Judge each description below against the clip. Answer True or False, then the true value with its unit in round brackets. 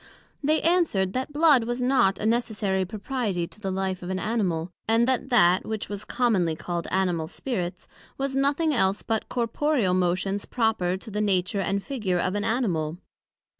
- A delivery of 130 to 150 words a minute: False (170 wpm)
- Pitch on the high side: True (205 Hz)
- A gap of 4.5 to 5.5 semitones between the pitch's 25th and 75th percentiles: True (4.9 semitones)